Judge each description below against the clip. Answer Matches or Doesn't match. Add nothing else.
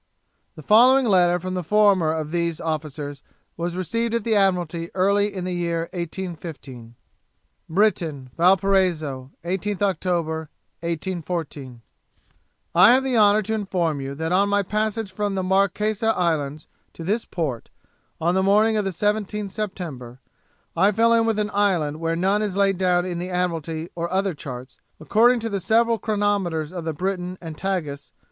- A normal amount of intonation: Matches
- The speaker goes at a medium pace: Matches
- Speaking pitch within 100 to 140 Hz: Doesn't match